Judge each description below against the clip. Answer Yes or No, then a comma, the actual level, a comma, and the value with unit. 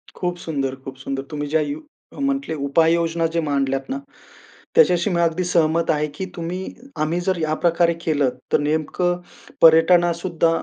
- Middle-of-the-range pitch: Yes, medium, 165 Hz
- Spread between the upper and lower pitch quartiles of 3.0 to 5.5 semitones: No, narrow, 2.5 semitones